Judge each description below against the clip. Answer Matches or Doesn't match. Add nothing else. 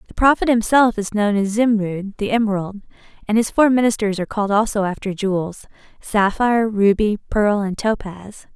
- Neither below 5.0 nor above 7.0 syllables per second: Matches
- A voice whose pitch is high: Matches